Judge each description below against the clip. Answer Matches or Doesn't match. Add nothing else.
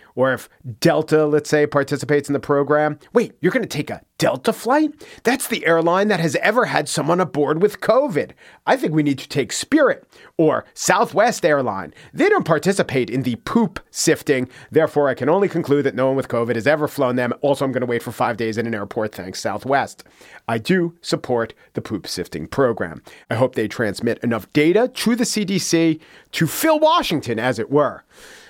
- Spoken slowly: Doesn't match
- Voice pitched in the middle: Matches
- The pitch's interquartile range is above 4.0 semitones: Matches